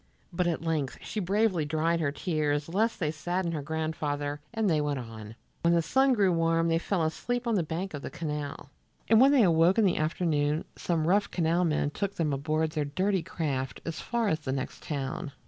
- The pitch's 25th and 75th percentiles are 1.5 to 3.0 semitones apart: No, average, 3.8 semitones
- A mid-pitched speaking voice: Yes, medium, 165 Hz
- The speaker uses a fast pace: Yes, fast, 210 wpm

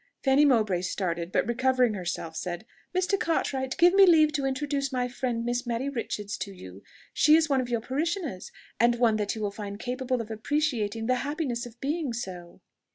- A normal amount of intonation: Yes, average, 4.9 semitones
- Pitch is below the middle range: No, high, 245 Hz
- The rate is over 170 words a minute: Yes, average, 190 wpm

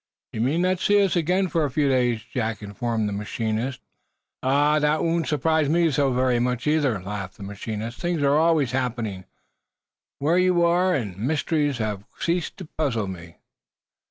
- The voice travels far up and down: Yes, wide, 6.4 semitones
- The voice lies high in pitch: No, low, 135 Hz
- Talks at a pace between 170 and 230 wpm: Yes, average, 180 wpm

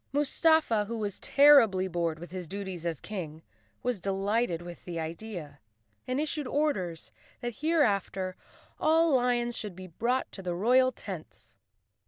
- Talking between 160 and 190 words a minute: No, average, 145 wpm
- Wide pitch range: Yes, wide, 6.5 semitones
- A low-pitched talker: No, high, 205 Hz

